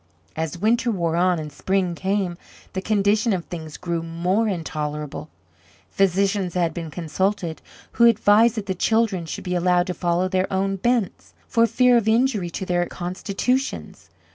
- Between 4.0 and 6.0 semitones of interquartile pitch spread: No, average, 3.6 semitones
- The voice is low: No, medium, 185 Hz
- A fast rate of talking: No, average, 160 wpm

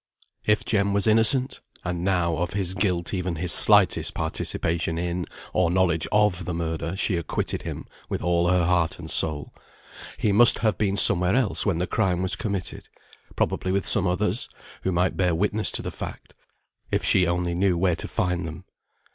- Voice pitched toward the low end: Yes, very low, 90 Hz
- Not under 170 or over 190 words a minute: Yes, average, 180 wpm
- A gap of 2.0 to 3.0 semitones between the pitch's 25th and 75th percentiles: Yes, narrow, 2.4 semitones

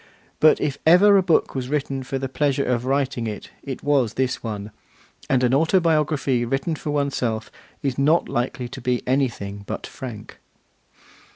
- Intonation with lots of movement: No, average, 3.0 semitones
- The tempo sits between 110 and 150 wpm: No, average, 165 wpm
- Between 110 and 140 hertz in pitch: Yes, low, 135 Hz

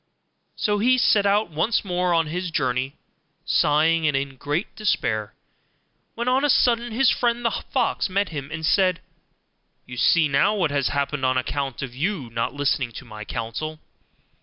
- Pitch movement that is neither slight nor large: No, wide, 7.0 semitones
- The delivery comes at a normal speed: Yes, average, 170 wpm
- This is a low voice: No, medium, 155 Hz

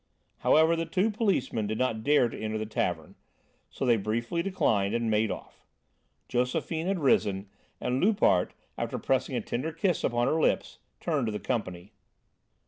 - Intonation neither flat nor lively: No, wide, 7.0 semitones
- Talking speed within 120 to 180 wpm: Yes, average, 165 wpm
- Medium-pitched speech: No, low, 120 Hz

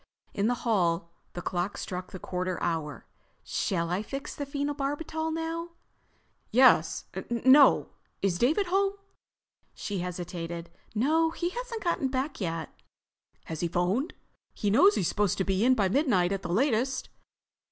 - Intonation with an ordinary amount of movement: No, wide, 8.4 semitones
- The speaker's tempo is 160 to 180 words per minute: No, average, 140 wpm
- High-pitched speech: Yes, high, 215 Hz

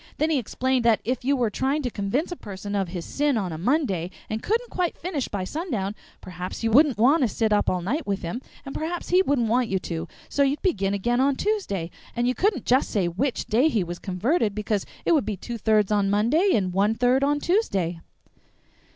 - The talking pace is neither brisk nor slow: No, fast, 225 wpm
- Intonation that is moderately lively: No, wide, 6.4 semitones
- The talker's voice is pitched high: Yes, high, 235 Hz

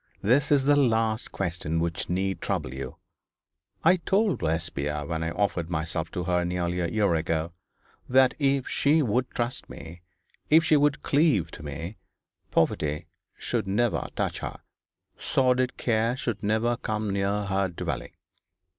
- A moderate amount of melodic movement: No, wide, 7.2 semitones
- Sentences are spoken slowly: No, average, 150 wpm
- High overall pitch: No, low, 100 Hz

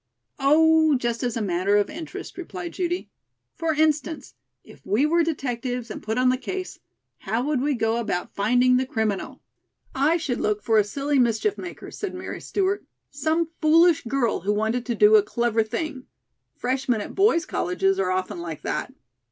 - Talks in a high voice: Yes, very high, 255 Hz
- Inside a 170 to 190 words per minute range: Yes, average, 175 wpm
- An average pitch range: No, wide, 6.4 semitones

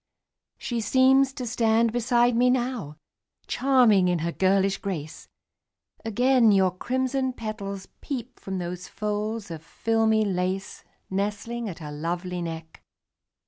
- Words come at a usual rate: No, slow, 125 wpm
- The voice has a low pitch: No, high, 215 Hz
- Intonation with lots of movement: No, average, 4.8 semitones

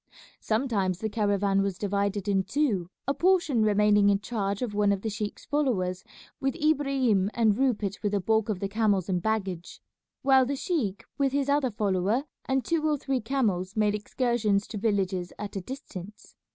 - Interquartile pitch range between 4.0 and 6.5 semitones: Yes, average, 4.7 semitones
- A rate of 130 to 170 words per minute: No, average, 180 wpm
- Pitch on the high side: Yes, high, 210 Hz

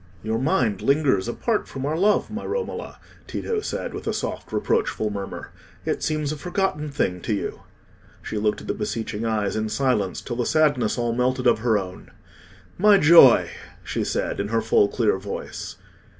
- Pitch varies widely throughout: Yes, wide, 6.2 semitones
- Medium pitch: No, low, 120 Hz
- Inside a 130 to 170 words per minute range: No, average, 180 wpm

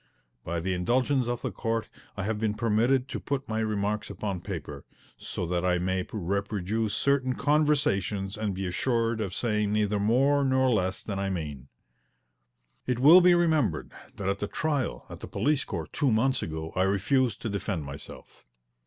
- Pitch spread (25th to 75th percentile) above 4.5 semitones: Yes, wide, 5.4 semitones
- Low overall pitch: Yes, low, 105 Hz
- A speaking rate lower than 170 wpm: No, average, 175 wpm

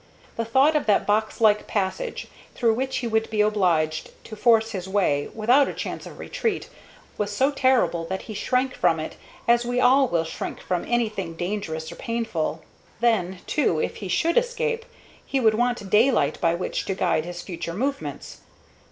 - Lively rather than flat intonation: Yes, wide, 5.8 semitones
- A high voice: Yes, high, 215 Hz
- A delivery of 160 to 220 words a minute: Yes, average, 180 wpm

